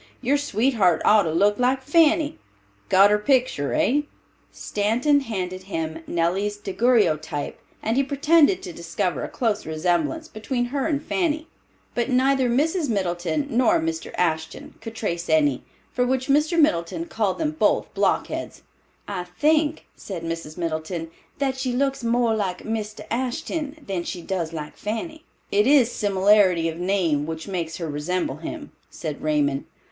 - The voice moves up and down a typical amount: No, wide, 8.1 semitones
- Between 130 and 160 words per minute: Yes, average, 150 wpm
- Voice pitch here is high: Yes, high, 210 Hz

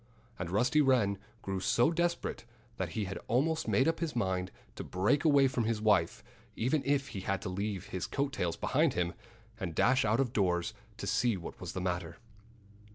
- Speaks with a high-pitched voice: No, low, 110 Hz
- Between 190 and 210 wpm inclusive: Yes, average, 195 wpm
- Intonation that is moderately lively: No, wide, 6.6 semitones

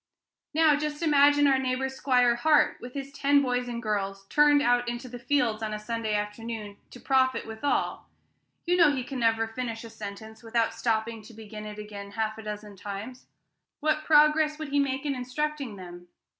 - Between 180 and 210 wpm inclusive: Yes, average, 185 wpm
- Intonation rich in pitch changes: No, average, 4.5 semitones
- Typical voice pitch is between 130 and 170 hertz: No, high, 240 Hz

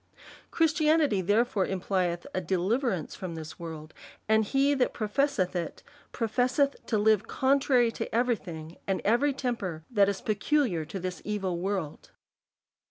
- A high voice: Yes, high, 210 Hz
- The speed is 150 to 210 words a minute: No, slow, 135 wpm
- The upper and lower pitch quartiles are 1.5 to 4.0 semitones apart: No, wide, 5.6 semitones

